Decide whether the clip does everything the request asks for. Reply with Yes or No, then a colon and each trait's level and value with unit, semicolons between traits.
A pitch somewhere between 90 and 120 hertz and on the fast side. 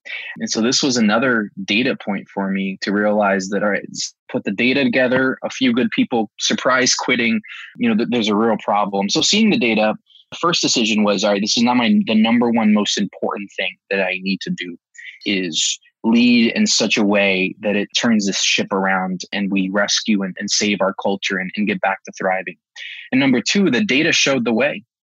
Yes: low, 110 Hz; fast, 215 wpm